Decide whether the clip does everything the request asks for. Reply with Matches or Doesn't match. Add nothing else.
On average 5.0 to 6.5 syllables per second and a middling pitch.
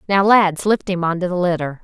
Matches